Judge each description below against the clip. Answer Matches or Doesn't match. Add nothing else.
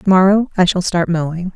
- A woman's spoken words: Matches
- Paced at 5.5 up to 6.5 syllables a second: Matches